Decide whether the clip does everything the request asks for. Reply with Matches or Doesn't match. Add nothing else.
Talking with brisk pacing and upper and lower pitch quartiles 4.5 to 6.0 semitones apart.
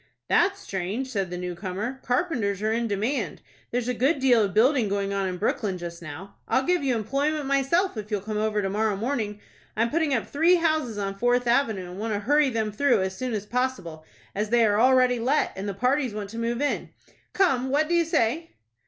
Matches